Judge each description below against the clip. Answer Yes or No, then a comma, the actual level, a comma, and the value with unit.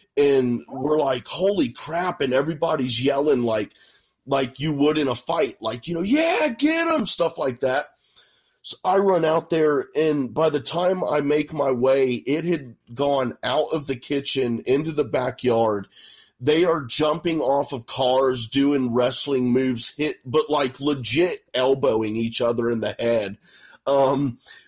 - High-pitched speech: No, medium, 140 Hz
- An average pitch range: Yes, average, 3.9 semitones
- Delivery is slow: No, average, 165 wpm